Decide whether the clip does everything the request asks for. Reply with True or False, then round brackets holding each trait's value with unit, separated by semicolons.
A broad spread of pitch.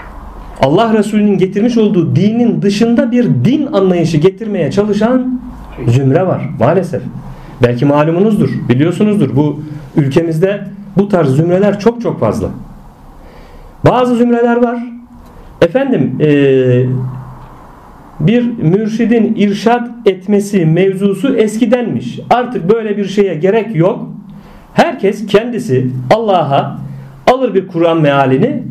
True (6.5 semitones)